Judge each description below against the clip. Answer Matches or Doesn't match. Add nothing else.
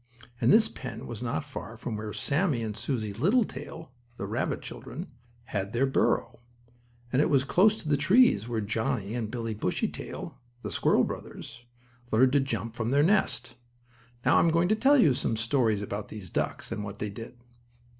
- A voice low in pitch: Matches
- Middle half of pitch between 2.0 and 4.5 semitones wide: Doesn't match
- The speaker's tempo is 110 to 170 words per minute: Doesn't match